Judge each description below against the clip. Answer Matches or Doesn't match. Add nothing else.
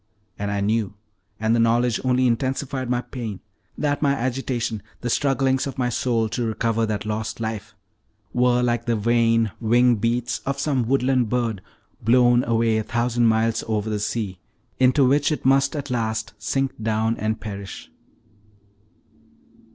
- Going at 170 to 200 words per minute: Doesn't match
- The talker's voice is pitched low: Matches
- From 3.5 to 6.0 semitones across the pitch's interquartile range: Doesn't match